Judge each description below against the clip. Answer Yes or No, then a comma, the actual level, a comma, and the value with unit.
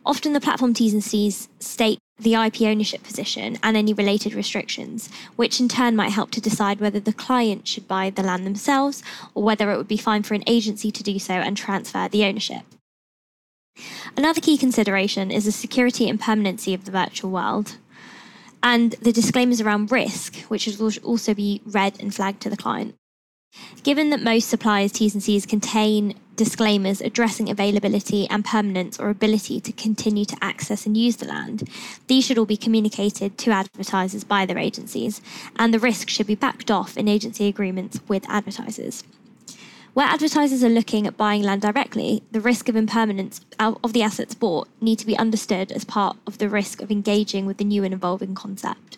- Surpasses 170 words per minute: Yes, average, 185 wpm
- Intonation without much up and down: Yes, narrow, 2.1 semitones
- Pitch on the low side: No, high, 215 Hz